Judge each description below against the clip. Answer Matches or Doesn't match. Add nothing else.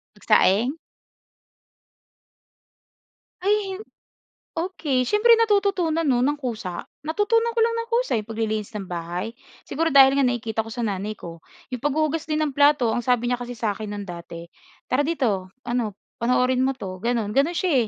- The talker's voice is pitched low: Doesn't match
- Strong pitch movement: Matches